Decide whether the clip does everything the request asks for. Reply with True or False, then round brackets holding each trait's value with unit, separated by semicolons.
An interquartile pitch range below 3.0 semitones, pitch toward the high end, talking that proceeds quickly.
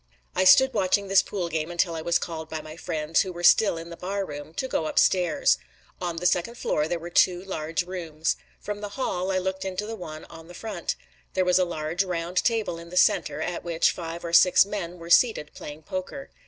False (2.4 semitones; 175 Hz; 225 wpm)